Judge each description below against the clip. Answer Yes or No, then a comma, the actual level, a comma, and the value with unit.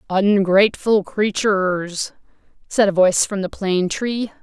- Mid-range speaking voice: No, high, 195 Hz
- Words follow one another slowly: Yes, slow, 120 wpm